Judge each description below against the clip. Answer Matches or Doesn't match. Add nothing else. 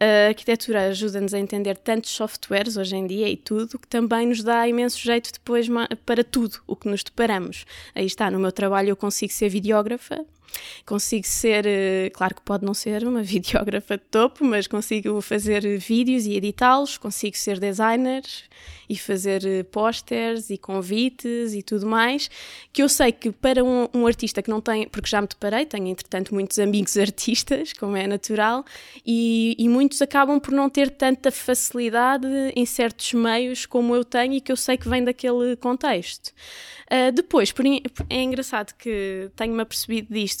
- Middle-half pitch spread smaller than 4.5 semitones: Matches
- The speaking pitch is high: Matches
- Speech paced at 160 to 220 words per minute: Matches